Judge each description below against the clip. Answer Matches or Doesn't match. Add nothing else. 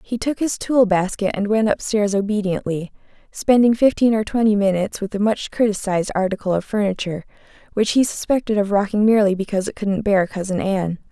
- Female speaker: Matches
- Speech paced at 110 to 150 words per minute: Doesn't match